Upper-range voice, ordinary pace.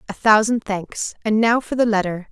Yes: high, 215 Hz; average, 180 wpm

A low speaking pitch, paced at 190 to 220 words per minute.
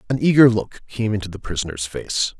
Yes: low, 105 Hz; average, 200 wpm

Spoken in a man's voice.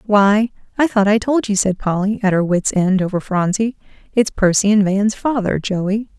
No: female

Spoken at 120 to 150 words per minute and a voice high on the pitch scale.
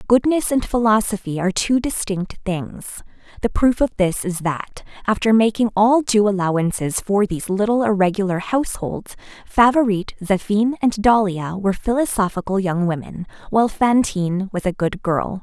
Yes: average, 145 wpm; high, 205 Hz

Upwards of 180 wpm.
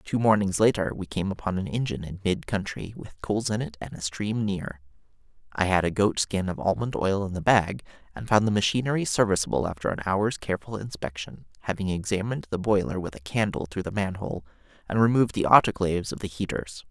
Yes: average, 200 wpm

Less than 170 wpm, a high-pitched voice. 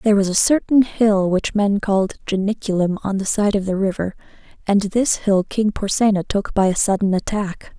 No: average, 195 wpm; high, 200 Hz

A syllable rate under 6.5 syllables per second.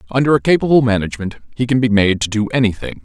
No: 7.0 syllables/s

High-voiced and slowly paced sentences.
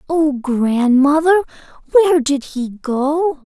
Yes: very high, 290 Hz; slow, 105 wpm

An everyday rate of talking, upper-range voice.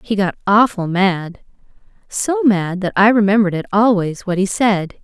Yes: average, 145 wpm; high, 200 Hz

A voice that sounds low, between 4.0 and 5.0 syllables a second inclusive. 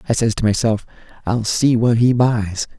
Yes: low, 115 Hz; 4.7 syllables/s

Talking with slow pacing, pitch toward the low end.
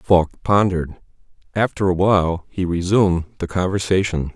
Yes: slow, 125 wpm; very low, 90 Hz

